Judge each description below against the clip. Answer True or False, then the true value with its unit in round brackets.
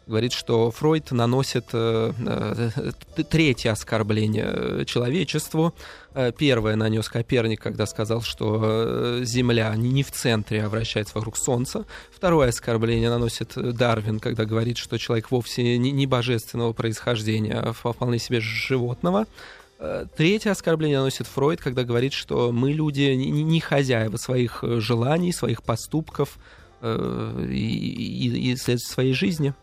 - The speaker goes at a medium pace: True (120 wpm)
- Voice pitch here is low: True (120 Hz)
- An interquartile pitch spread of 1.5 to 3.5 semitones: True (2.9 semitones)